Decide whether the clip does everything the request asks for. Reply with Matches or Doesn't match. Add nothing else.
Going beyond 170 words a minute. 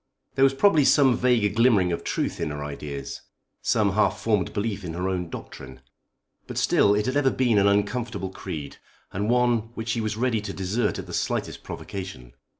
Matches